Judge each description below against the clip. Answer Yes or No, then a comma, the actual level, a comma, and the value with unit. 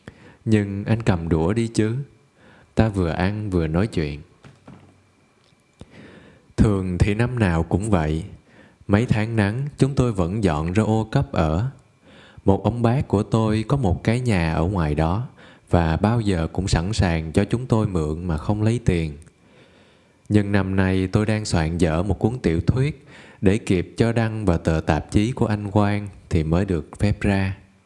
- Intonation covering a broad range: No, average, 4.0 semitones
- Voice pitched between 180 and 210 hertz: No, low, 100 Hz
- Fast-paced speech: No, average, 175 wpm